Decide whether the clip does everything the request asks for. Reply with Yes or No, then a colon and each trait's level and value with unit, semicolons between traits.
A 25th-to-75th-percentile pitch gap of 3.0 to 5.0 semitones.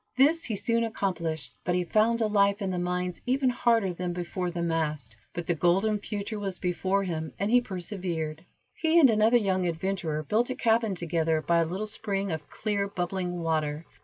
Yes: average, 4.1 semitones